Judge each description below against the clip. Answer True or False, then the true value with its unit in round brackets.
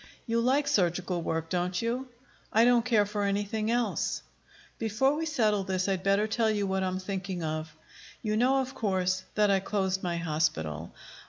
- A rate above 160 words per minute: True (175 wpm)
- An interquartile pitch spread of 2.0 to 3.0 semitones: False (3.9 semitones)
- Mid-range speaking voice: False (200 Hz)